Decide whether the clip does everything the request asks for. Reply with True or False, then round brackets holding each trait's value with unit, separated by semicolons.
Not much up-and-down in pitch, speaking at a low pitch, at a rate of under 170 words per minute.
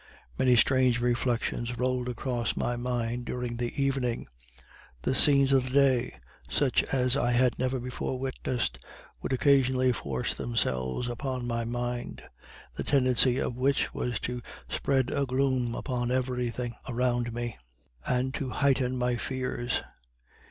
True (1.3 semitones; 125 Hz; 140 wpm)